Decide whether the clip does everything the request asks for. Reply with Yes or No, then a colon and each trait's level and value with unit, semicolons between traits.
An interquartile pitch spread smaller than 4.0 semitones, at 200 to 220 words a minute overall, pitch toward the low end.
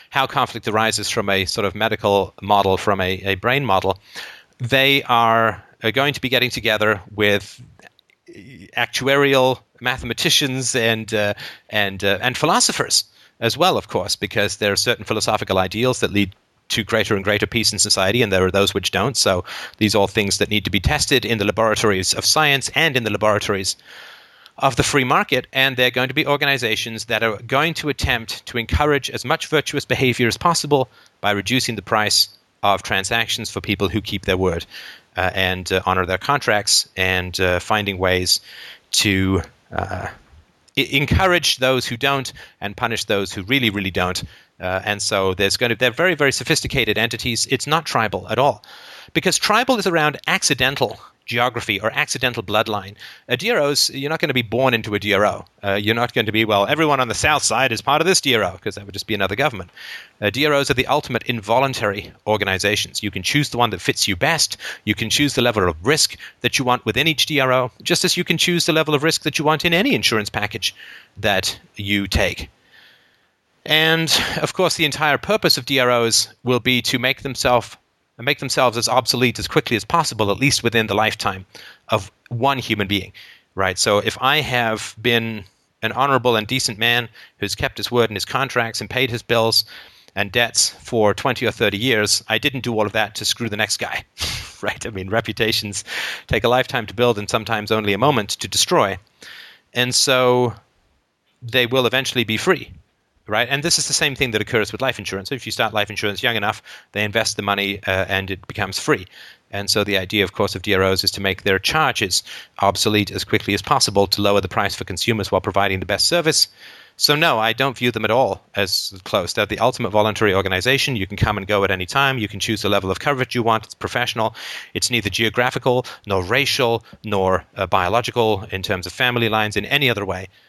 No: average, 4.3 semitones; fast, 205 wpm; low, 115 Hz